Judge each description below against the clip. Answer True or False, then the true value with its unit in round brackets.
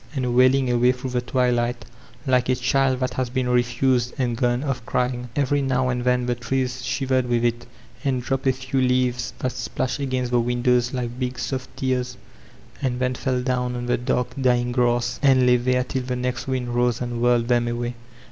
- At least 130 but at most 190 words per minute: False (200 wpm)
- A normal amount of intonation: False (1.0 semitones)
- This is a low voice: True (125 Hz)